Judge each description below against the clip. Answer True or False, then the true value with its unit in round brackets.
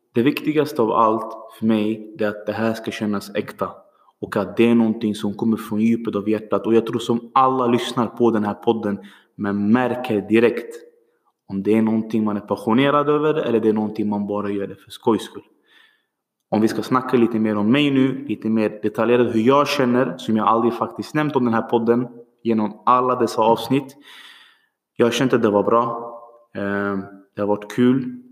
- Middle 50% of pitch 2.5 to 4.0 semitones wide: True (2.8 semitones)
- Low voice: True (115 Hz)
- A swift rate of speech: True (200 wpm)